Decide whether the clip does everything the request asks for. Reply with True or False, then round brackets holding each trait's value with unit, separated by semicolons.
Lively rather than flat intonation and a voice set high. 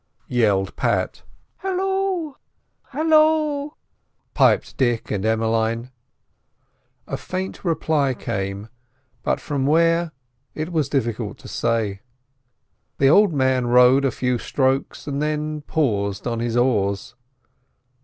False (6.5 semitones; 130 Hz)